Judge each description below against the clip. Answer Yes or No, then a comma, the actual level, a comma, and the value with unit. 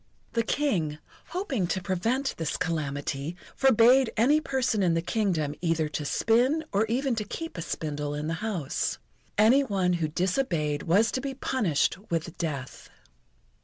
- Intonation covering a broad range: Yes, wide, 7.8 semitones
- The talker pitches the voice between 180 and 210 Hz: Yes, high, 190 Hz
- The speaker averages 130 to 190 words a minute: Yes, average, 155 wpm